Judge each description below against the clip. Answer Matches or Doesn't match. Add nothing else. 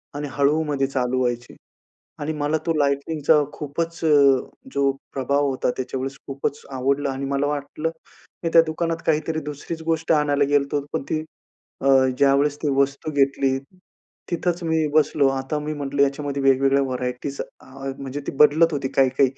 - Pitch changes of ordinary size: Doesn't match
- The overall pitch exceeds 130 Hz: Matches